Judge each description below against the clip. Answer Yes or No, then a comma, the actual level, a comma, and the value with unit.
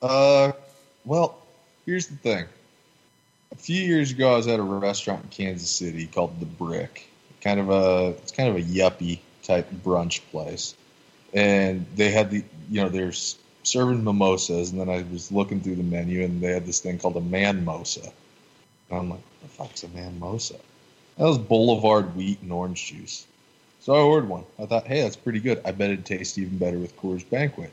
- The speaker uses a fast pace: No, average, 195 wpm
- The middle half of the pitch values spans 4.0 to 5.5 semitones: Yes, average, 4.4 semitones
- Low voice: Yes, low, 100 Hz